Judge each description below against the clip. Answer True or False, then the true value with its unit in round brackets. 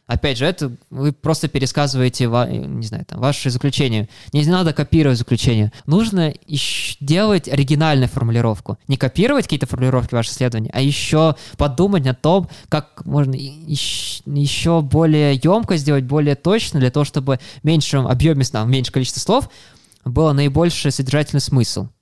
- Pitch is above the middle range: False (140 Hz)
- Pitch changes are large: False (3.5 semitones)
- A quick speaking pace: False (150 wpm)